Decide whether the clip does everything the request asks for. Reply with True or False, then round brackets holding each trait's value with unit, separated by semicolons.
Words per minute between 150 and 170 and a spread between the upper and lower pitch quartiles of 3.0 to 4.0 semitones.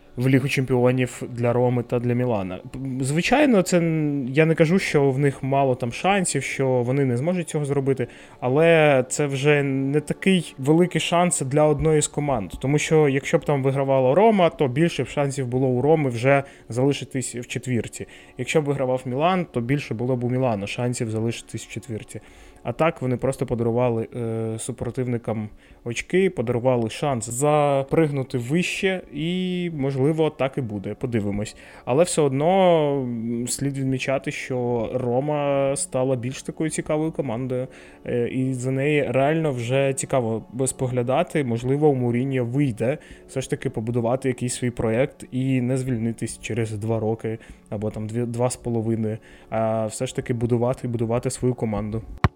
True (155 wpm; 3.4 semitones)